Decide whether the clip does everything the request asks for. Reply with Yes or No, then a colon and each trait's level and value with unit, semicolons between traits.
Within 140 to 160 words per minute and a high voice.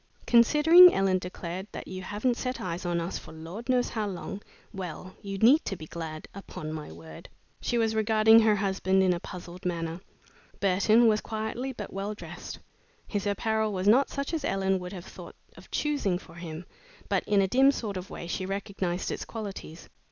No: average, 190 wpm; high, 195 Hz